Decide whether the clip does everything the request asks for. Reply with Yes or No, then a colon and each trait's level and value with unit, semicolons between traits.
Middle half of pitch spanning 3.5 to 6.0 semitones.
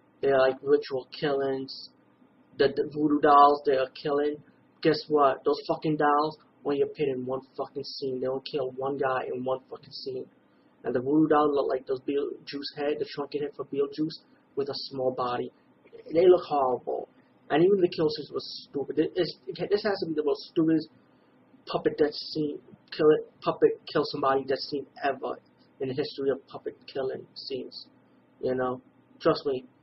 No: average, 3.0 semitones